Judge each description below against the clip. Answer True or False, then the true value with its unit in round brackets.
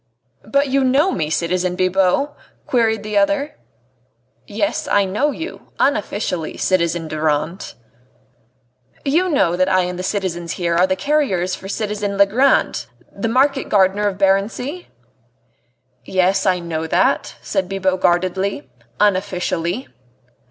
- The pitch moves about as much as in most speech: True (3.9 semitones)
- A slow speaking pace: True (125 wpm)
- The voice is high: True (195 Hz)